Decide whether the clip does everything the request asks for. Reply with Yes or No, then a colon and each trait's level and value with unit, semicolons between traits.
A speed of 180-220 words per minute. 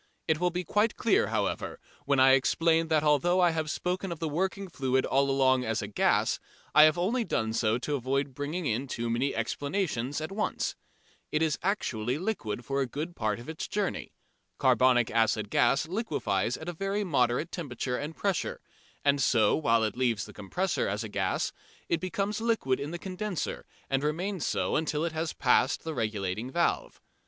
Yes: average, 185 wpm